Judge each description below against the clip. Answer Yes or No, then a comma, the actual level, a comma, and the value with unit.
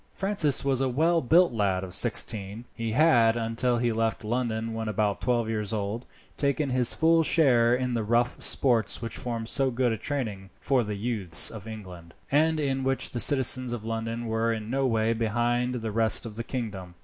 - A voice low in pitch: Yes, low, 115 Hz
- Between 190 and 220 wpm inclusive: Yes, average, 195 wpm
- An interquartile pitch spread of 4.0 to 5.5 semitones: No, narrow, 2.6 semitones